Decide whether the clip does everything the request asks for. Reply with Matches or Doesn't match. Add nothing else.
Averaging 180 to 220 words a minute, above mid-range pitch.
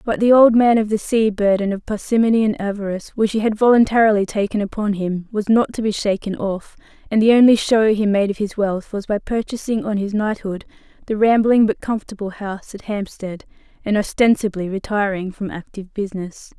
Matches